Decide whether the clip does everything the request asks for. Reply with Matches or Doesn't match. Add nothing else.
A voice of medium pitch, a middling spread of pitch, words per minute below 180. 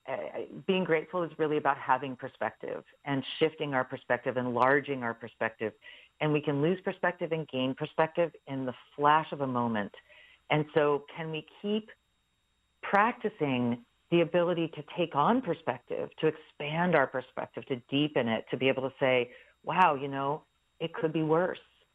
Matches